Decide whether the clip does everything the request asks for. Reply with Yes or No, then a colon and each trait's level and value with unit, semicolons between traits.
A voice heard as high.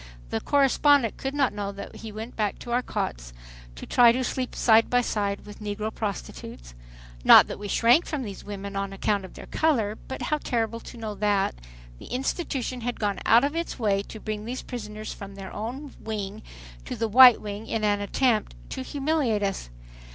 Yes: high, 220 Hz